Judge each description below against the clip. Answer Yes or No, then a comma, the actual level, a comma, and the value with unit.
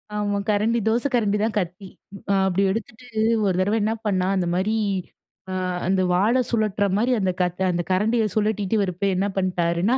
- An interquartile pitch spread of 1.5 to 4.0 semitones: Yes, average, 2.8 semitones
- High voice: Yes, high, 200 Hz